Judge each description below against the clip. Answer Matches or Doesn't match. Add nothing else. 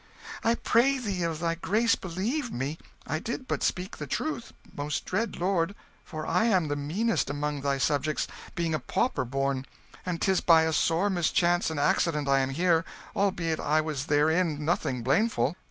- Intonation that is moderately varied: Matches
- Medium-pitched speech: Matches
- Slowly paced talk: Doesn't match